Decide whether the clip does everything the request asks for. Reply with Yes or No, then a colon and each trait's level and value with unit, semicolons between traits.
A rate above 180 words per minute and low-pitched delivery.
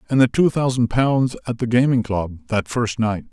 Yes: average, 200 wpm; low, 120 Hz